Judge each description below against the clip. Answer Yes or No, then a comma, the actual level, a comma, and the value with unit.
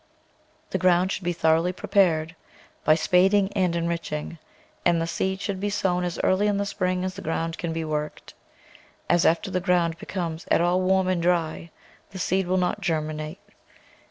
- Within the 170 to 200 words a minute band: Yes, average, 180 wpm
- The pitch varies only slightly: Yes, narrow, 2.3 semitones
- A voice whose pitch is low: No, medium, 175 Hz